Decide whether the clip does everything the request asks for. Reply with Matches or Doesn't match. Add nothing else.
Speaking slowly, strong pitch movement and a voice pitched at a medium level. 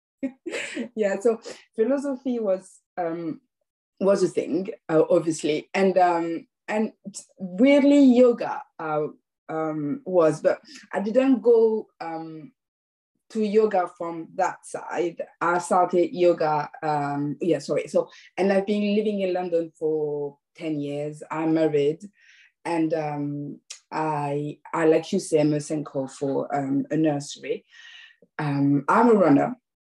Matches